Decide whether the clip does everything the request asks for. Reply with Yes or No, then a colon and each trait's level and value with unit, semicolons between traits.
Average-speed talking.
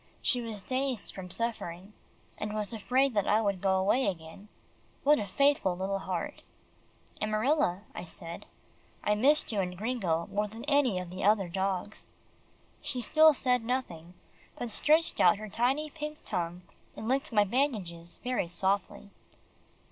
Yes: average, 155 wpm